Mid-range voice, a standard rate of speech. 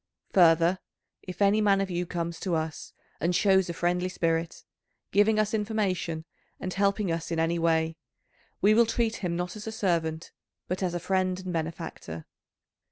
Yes: medium, 180 Hz; average, 170 wpm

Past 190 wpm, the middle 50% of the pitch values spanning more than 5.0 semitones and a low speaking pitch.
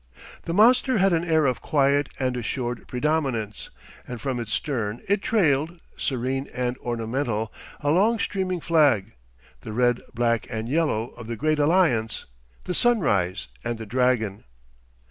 No: average, 145 wpm; wide, 5.6 semitones; low, 130 Hz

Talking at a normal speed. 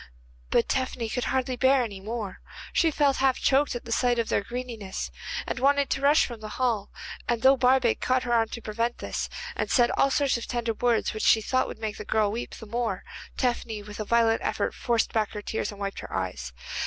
No: fast, 225 wpm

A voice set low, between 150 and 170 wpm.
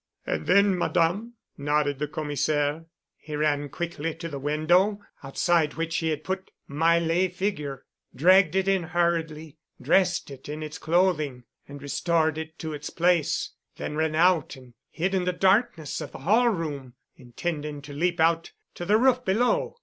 No: medium, 160 Hz; average, 165 wpm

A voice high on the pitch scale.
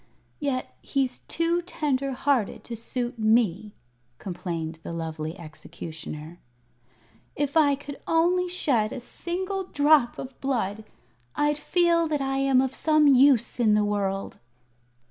Yes: very high, 260 Hz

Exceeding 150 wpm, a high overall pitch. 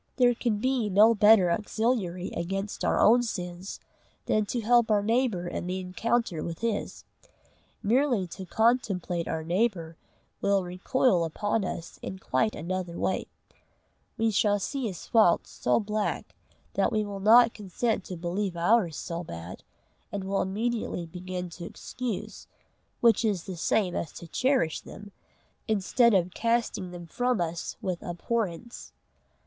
No: average, 145 wpm; high, 200 Hz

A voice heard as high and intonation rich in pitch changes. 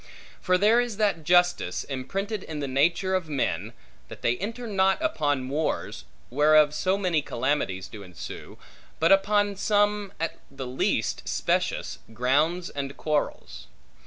No: medium, 165 Hz; wide, 6.1 semitones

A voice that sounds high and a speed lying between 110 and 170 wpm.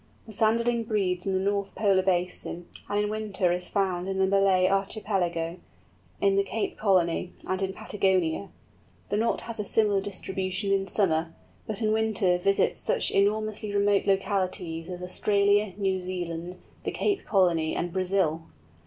Yes: high, 195 Hz; average, 155 wpm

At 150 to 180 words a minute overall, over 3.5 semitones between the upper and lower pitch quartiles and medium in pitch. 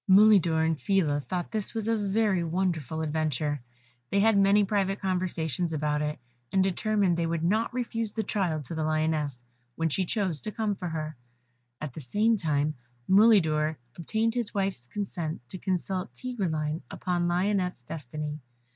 Yes: average, 160 wpm; average, 4.6 semitones; medium, 175 Hz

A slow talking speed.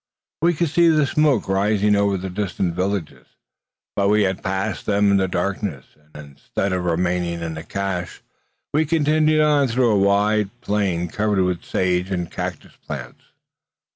No: average, 160 wpm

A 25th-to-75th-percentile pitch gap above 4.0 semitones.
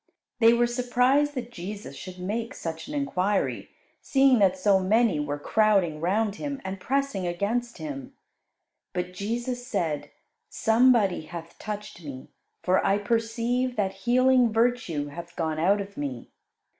Yes: wide, 5.6 semitones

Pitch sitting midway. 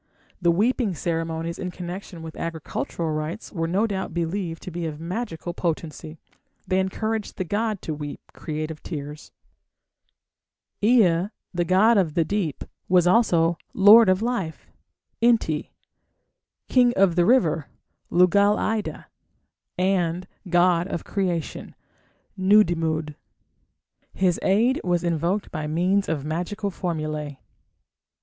Yes: medium, 175 Hz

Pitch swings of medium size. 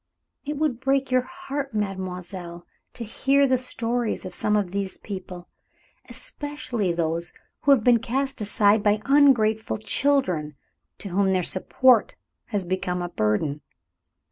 No: wide, 6.2 semitones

